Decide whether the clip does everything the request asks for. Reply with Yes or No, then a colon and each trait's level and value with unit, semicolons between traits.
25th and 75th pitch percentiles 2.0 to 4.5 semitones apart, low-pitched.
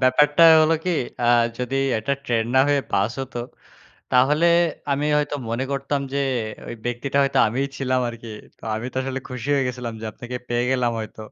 Yes: narrow, 2.6 semitones; low, 130 Hz